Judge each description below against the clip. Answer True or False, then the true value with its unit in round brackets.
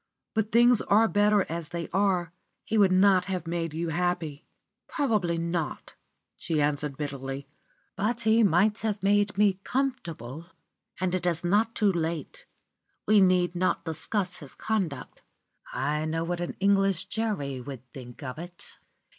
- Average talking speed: True (150 wpm)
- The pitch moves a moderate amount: True (4.3 semitones)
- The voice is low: False (180 Hz)